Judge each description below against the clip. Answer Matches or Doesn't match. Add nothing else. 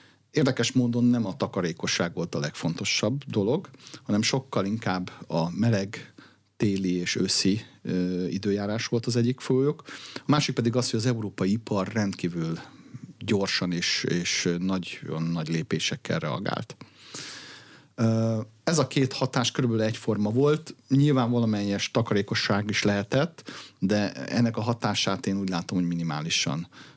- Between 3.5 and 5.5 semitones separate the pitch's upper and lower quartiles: Matches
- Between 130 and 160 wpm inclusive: Matches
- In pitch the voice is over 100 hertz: Matches